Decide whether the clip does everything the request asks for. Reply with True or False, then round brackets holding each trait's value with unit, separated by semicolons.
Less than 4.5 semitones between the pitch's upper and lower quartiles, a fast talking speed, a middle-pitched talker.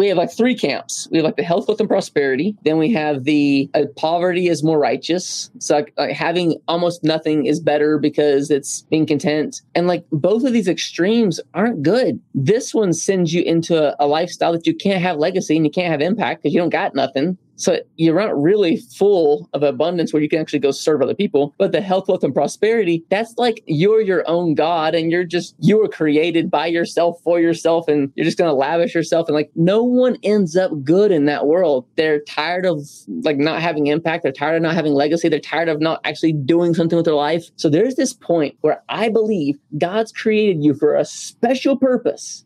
True (3.6 semitones; 220 wpm; 165 Hz)